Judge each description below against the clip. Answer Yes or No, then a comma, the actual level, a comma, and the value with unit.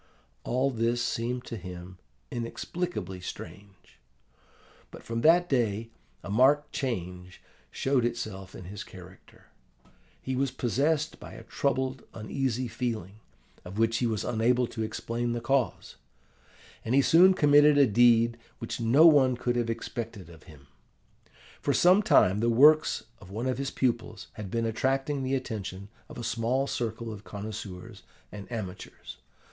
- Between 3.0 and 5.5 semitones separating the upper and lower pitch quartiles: Yes, average, 4.0 semitones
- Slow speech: No, average, 150 wpm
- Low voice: Yes, low, 115 Hz